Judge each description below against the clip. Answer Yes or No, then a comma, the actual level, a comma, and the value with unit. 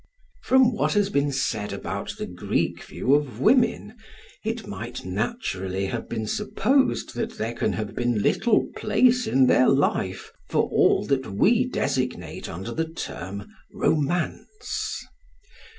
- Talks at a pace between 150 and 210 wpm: No, slow, 135 wpm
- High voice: No, medium, 140 Hz